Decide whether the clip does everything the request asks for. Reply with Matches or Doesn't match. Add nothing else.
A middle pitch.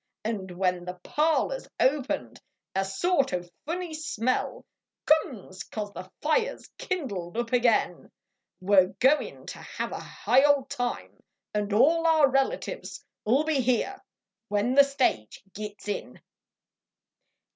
Doesn't match